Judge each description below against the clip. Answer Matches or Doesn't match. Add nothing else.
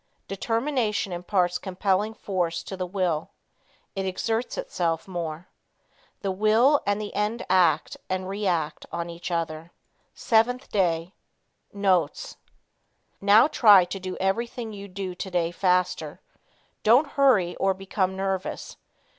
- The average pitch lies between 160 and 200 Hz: Matches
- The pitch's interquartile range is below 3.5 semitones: Matches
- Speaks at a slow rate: Matches